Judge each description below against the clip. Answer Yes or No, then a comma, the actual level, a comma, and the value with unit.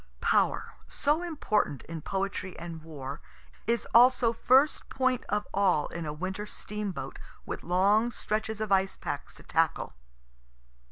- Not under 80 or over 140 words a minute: Yes, slow, 135 wpm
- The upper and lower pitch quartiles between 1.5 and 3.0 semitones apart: No, average, 4.9 semitones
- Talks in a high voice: Yes, high, 205 Hz